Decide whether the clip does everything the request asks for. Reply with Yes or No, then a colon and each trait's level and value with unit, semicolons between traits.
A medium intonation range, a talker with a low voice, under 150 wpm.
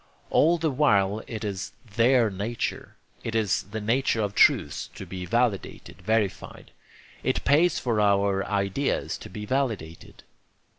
Yes: average, 4.0 semitones; low, 110 Hz; average, 140 wpm